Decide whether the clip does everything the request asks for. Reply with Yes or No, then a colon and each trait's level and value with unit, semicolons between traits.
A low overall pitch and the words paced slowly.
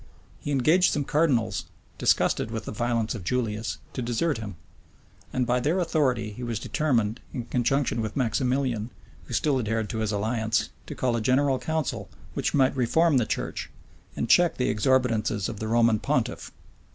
No: low, 120 Hz; average, 170 wpm